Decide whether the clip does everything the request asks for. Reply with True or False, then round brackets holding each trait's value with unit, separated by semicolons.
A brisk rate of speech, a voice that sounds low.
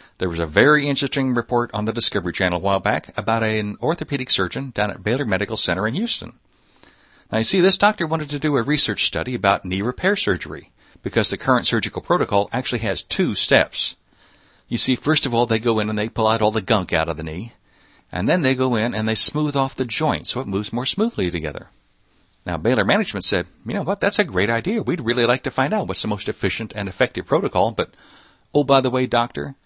True (230 wpm; 115 Hz)